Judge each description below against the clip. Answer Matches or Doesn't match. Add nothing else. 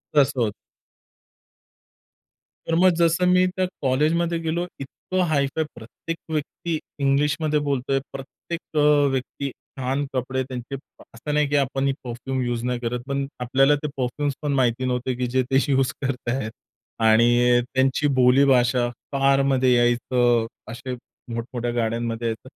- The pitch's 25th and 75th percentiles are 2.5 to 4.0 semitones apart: Matches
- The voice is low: Matches